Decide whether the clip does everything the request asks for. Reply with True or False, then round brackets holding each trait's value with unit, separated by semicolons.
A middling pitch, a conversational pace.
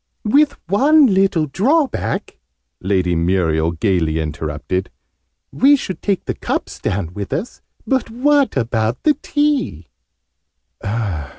False (145 Hz; 110 wpm)